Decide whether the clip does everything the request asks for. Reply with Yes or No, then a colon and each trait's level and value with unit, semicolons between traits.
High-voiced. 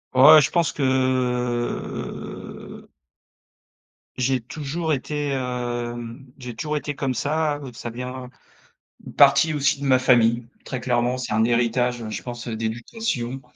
No: low, 125 Hz